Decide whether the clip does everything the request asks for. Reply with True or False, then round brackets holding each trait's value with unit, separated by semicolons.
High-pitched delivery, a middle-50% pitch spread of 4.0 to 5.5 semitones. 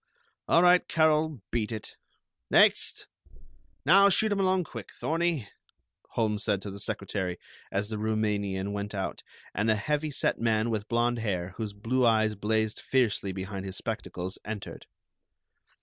False (110 Hz; 4.5 semitones)